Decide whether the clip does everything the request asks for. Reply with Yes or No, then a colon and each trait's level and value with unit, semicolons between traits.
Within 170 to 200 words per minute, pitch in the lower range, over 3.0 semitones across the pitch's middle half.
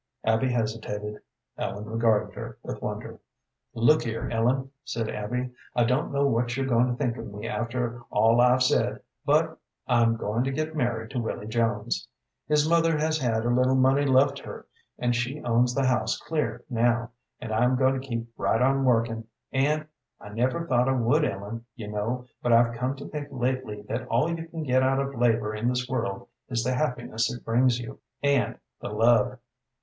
No: average, 190 wpm; low, 120 Hz; narrow, 2.5 semitones